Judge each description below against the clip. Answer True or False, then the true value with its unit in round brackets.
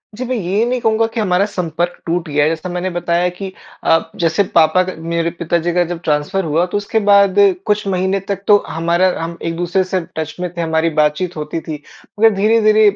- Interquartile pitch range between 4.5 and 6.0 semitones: False (3.2 semitones)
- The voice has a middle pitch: True (180 Hz)